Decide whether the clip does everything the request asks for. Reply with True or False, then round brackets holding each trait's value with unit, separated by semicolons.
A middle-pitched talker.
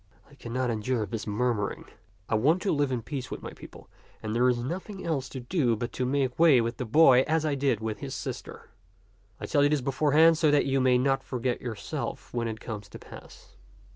False (130 Hz)